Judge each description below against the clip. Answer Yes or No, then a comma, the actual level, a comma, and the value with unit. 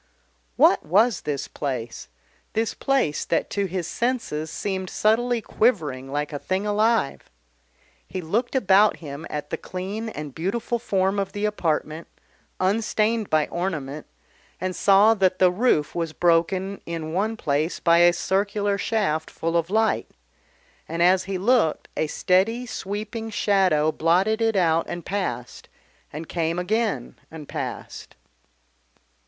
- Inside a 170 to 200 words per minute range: No, average, 140 wpm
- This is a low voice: No, medium, 185 Hz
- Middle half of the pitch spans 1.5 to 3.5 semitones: No, average, 4.9 semitones